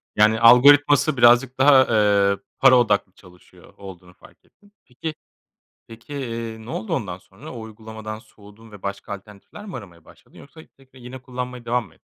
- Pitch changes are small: No, average, 3.9 semitones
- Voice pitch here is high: No, low, 115 Hz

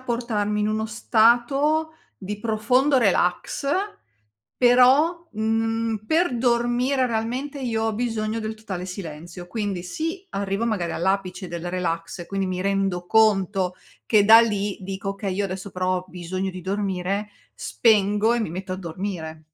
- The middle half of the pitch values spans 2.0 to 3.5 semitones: No, average, 4.0 semitones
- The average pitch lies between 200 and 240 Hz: Yes, high, 210 Hz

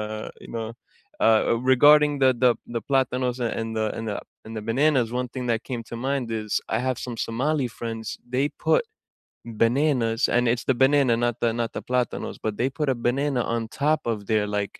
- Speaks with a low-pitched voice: Yes, low, 120 Hz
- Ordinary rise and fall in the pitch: Yes, average, 3.0 semitones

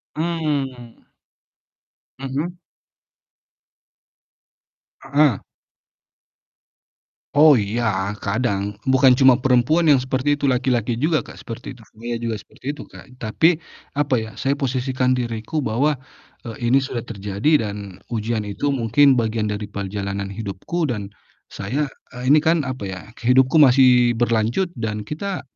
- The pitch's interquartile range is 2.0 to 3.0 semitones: No, average, 4.2 semitones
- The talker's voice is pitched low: Yes, low, 125 Hz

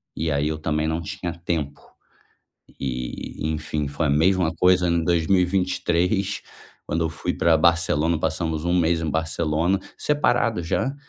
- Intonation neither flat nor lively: No, narrow, 2.3 semitones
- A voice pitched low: Yes, very low, 80 Hz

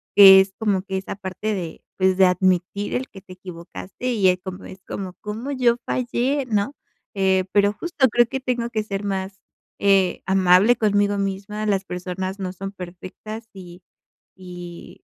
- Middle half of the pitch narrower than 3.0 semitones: Yes, narrow, 2.5 semitones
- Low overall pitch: No, high, 195 Hz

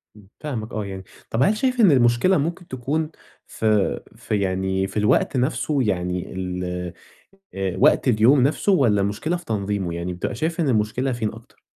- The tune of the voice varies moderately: No, wide, 6.6 semitones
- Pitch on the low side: Yes, low, 110 Hz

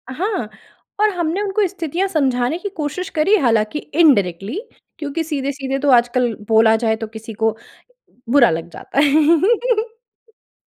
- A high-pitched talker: Yes, very high, 290 Hz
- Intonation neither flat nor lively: No, wide, 8.0 semitones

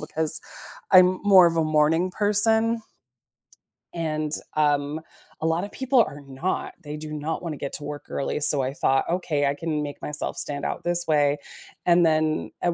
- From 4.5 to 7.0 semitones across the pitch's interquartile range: No, average, 3.2 semitones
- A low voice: No, medium, 155 Hz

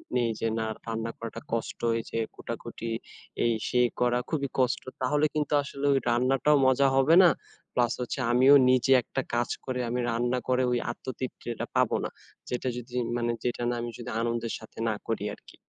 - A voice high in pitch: No, low, 125 Hz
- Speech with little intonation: Yes, narrow, 1.8 semitones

